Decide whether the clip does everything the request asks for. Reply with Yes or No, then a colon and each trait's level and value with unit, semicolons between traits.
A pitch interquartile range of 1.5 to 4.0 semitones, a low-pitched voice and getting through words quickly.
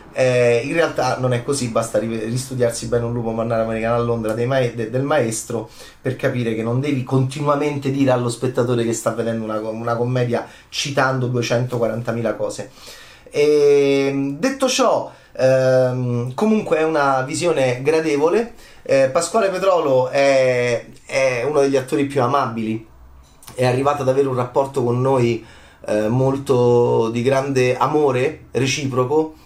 No: average, 2.9 semitones; low, 125 Hz; average, 145 wpm